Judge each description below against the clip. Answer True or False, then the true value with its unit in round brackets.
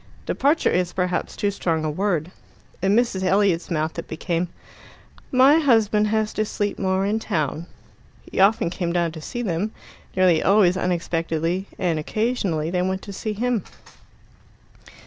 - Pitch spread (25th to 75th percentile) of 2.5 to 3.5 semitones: False (3.9 semitones)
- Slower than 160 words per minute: True (150 wpm)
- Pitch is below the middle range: False (190 Hz)